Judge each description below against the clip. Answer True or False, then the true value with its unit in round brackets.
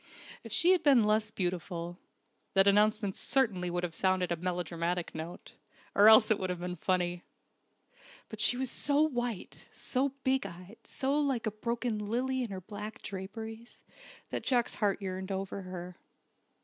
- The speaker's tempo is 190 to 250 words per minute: False (160 wpm)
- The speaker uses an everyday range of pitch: True (4.7 semitones)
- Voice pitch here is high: True (205 Hz)